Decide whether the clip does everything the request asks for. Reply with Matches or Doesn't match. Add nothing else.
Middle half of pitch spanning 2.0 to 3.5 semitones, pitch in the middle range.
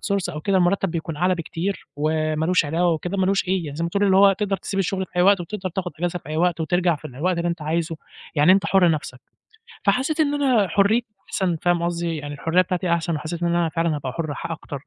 Matches